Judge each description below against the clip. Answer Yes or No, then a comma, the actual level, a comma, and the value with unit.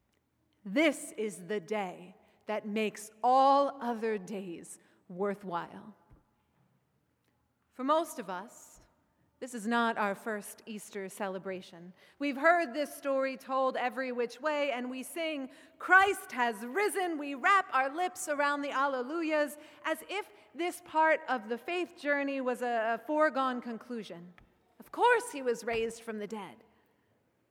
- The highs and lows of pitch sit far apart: Yes, wide, 6.0 semitones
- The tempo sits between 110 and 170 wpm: Yes, slow, 135 wpm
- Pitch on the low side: No, very high, 255 Hz